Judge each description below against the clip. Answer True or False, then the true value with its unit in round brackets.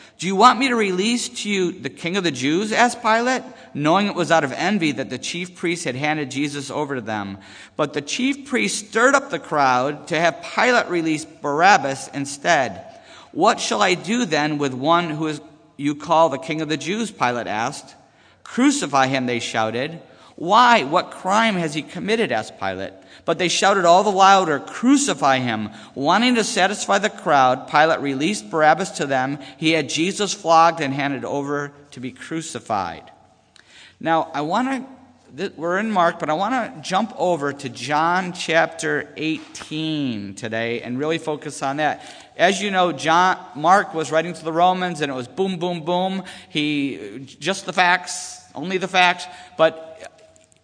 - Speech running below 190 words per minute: True (180 wpm)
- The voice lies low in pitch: False (165 Hz)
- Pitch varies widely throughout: False (5.0 semitones)